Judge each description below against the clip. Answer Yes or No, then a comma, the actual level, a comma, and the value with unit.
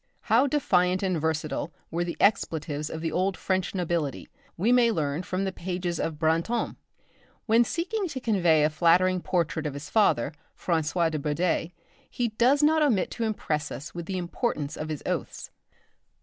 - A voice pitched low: No, medium, 175 Hz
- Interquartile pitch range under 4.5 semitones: No, wide, 5.4 semitones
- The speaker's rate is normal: Yes, average, 170 wpm